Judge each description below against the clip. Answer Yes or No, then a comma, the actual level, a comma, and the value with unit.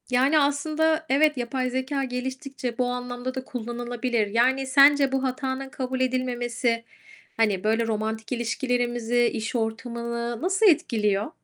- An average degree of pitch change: No, narrow, 2.3 semitones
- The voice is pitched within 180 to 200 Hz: No, very high, 250 Hz